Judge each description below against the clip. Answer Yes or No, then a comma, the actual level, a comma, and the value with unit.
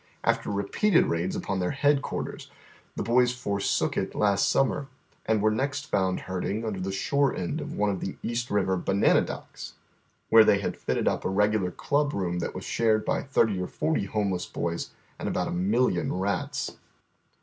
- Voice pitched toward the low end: Yes, low, 105 Hz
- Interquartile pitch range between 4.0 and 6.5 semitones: Yes, average, 4.4 semitones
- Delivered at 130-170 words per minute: No, average, 185 wpm